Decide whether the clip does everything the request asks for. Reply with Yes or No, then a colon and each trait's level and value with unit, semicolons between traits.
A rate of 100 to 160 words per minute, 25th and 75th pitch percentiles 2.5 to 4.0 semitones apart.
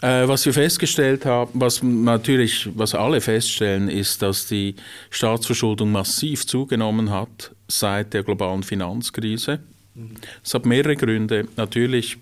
Yes: slow, 125 wpm; average, 3.0 semitones